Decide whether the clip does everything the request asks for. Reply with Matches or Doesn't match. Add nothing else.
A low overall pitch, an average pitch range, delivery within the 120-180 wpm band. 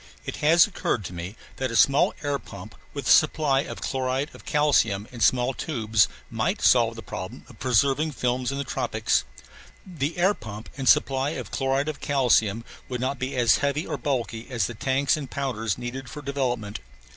Doesn't match